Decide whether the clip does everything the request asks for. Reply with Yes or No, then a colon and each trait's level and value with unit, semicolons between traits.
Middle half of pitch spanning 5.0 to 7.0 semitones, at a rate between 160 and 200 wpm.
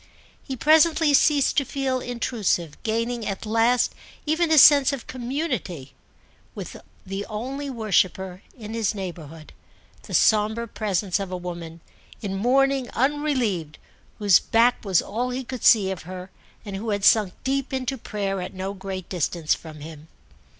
No: wide, 5.6 semitones; average, 150 wpm